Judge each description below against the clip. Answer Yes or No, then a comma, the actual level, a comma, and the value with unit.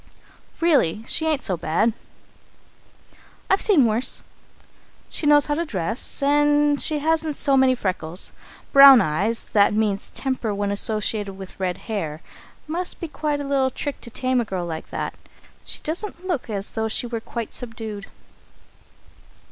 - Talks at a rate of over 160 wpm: No, average, 155 wpm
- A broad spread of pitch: Yes, wide, 6.3 semitones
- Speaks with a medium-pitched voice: No, high, 240 Hz